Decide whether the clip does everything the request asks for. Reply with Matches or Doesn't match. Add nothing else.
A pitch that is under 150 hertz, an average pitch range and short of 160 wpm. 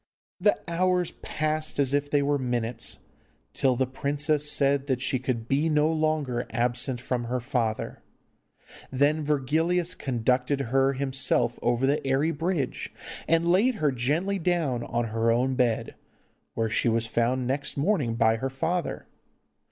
Matches